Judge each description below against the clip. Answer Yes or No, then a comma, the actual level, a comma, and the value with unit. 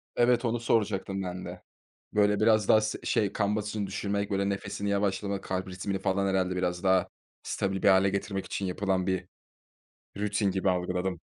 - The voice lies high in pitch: No, low, 100 Hz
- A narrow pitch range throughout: Yes, narrow, 1.6 semitones